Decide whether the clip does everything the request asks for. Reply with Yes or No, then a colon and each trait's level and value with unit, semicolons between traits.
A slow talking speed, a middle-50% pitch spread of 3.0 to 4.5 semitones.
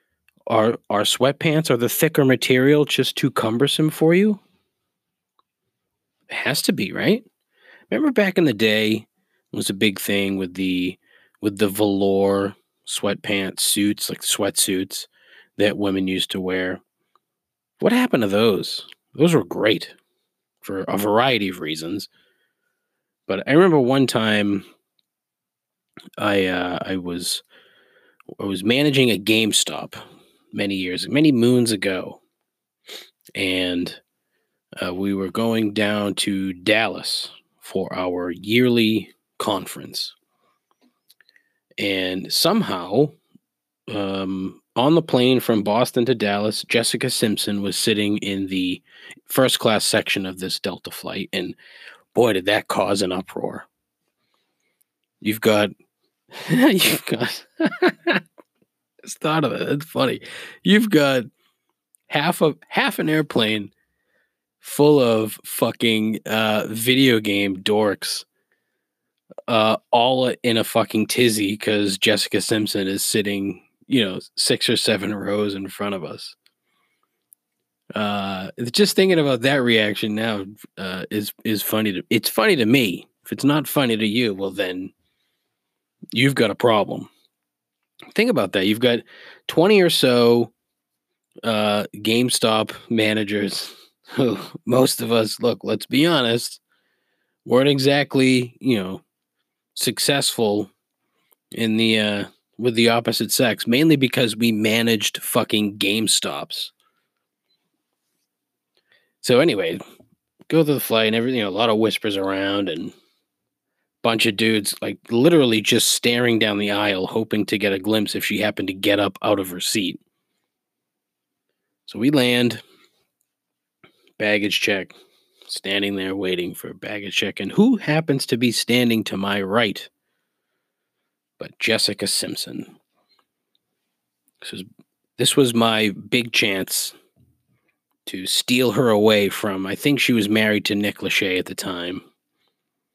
Yes: slow, 130 wpm; average, 3.7 semitones